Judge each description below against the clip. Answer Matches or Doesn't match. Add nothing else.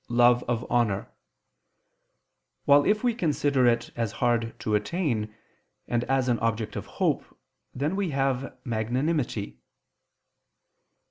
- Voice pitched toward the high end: Doesn't match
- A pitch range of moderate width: Matches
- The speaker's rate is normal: Doesn't match